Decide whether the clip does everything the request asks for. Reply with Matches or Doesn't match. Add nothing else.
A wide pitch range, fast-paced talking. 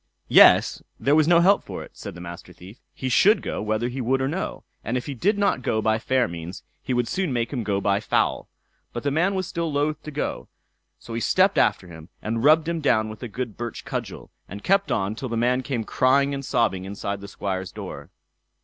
Matches